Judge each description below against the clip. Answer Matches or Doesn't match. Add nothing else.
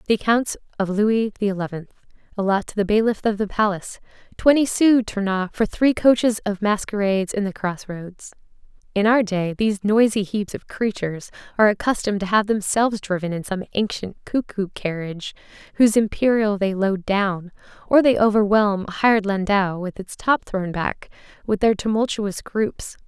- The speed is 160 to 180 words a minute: Matches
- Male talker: Doesn't match